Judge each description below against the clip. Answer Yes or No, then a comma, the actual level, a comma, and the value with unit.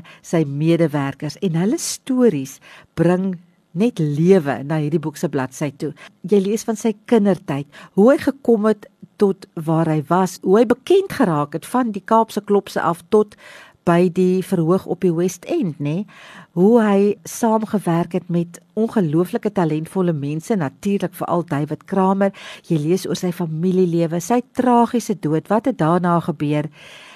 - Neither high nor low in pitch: Yes, medium, 180 Hz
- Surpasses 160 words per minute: No, average, 155 wpm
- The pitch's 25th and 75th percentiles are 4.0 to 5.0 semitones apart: Yes, average, 4.3 semitones